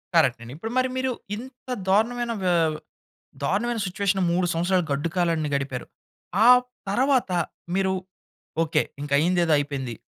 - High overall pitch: No, medium, 180 Hz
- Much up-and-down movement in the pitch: Yes, wide, 6.9 semitones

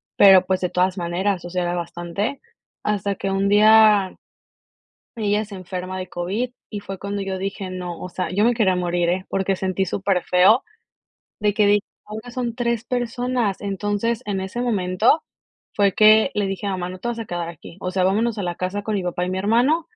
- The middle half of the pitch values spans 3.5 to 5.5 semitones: No, average, 2.8 semitones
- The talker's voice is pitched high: Yes, high, 195 Hz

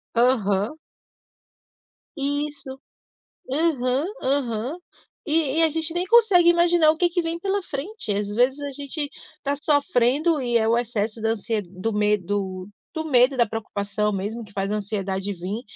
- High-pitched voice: Yes, very high, 255 Hz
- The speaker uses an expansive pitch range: Yes, wide, 6.8 semitones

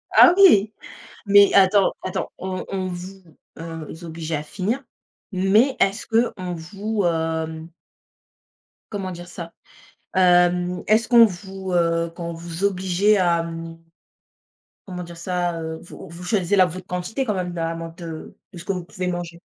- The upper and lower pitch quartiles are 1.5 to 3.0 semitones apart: Yes, narrow, 2.6 semitones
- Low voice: No, medium, 180 Hz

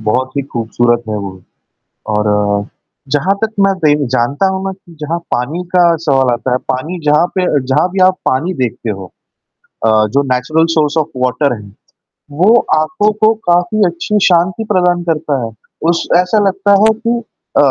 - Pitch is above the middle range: No, medium, 155 Hz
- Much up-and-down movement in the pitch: Yes, wide, 6.3 semitones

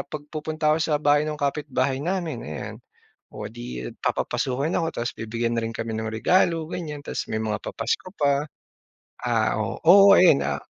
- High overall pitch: No, medium, 140 Hz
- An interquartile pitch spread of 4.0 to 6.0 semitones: Yes, wide, 5.6 semitones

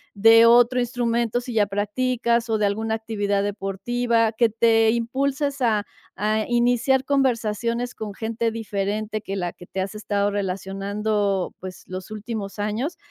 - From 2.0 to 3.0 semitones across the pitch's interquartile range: Yes, average, 2.7 semitones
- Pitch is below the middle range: No, high, 220 Hz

